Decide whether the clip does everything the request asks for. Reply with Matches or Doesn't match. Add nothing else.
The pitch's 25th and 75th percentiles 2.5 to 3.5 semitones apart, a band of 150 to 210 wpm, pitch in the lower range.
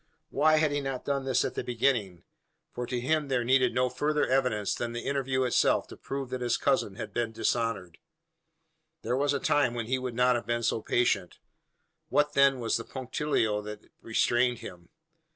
Matches